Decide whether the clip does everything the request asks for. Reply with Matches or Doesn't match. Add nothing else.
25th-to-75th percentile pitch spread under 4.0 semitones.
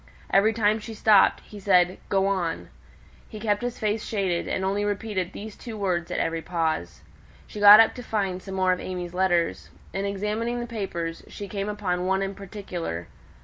Matches